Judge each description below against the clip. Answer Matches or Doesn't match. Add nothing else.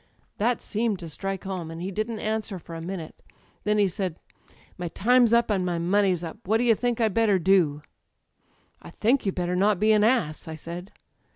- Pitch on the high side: Matches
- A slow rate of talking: Doesn't match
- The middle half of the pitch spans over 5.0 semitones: Doesn't match